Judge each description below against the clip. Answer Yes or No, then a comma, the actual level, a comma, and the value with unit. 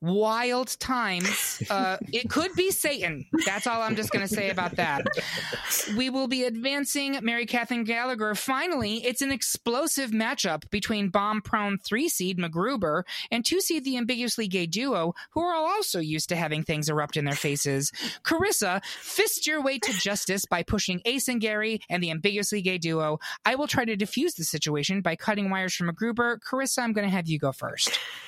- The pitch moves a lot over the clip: Yes, wide, 5.8 semitones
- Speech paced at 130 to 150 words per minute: No, average, 185 wpm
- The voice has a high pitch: Yes, high, 220 Hz